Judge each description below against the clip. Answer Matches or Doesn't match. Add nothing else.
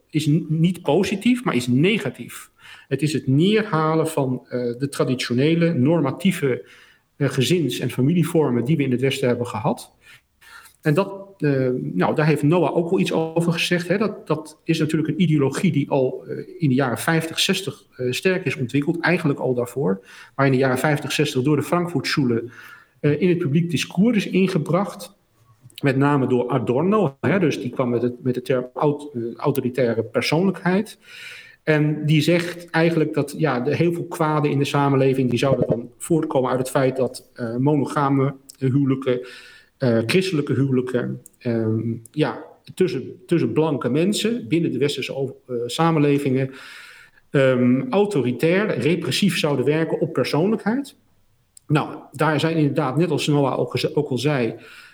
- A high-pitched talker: Doesn't match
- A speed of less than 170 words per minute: Matches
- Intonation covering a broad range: Doesn't match